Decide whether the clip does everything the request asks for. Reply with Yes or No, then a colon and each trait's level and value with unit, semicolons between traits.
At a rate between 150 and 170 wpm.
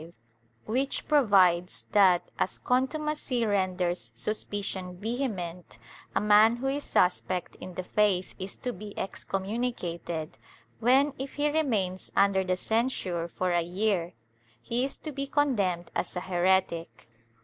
No: slow, 135 wpm